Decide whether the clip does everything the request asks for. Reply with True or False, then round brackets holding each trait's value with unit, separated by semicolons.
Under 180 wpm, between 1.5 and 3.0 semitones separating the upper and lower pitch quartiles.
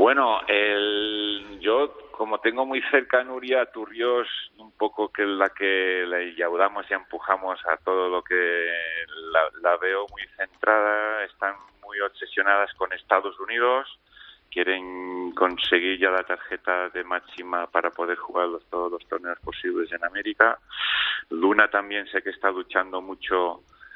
True (150 wpm; 2.7 semitones)